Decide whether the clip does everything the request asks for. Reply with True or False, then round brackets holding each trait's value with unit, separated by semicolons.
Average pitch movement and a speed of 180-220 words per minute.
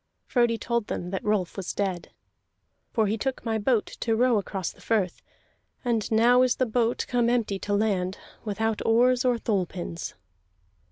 False (3.1 semitones; 170 wpm)